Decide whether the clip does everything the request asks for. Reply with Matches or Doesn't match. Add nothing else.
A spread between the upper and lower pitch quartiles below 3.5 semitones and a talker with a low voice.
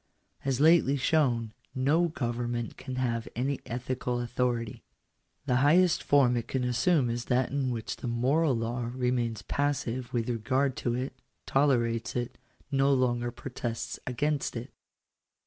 Matches